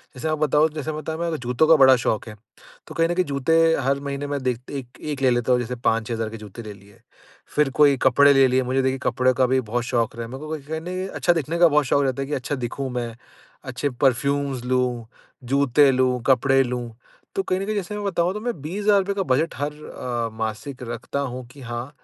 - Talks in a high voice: No, low, 135 Hz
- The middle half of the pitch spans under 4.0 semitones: Yes, average, 3.5 semitones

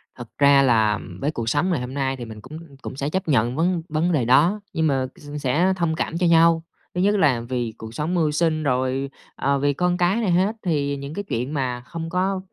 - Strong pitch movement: No, average, 4.7 semitones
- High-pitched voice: No, medium, 145 Hz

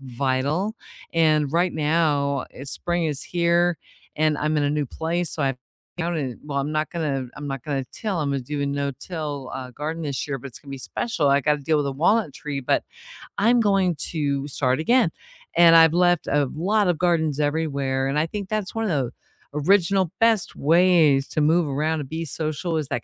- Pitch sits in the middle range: Yes, medium, 155 Hz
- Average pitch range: Yes, average, 3.5 semitones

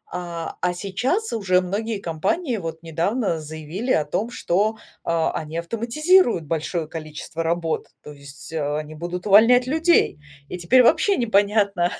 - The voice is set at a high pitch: No, medium, 180 Hz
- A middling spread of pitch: No, wide, 6.0 semitones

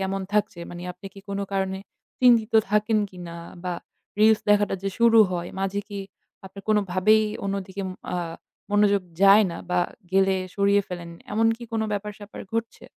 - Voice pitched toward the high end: Yes, high, 200 Hz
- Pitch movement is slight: Yes, narrow, 1.8 semitones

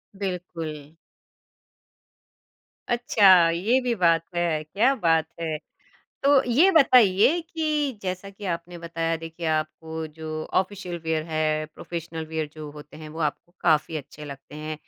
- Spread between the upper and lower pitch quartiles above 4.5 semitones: No, average, 4.1 semitones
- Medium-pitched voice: Yes, medium, 170 Hz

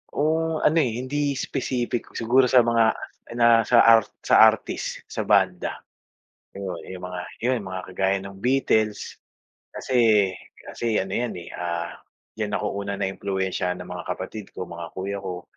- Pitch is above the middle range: No, low, 110 Hz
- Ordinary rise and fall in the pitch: Yes, average, 4.3 semitones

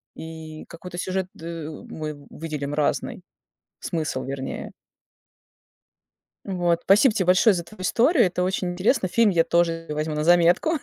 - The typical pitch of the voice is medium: Yes, medium, 170 Hz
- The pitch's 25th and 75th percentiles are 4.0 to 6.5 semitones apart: No, average, 2.9 semitones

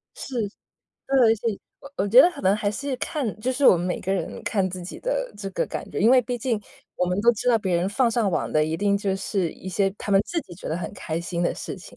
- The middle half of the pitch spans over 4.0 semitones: Yes, average, 5.0 semitones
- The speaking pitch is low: No, high, 205 Hz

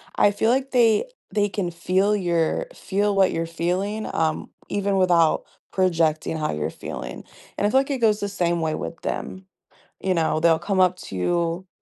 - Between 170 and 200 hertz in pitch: Yes, medium, 185 Hz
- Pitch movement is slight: No, average, 3.6 semitones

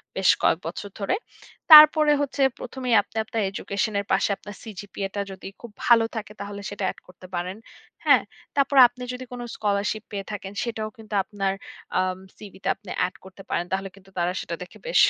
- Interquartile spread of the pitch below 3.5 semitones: Yes, average, 2.8 semitones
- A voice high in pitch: Yes, high, 205 Hz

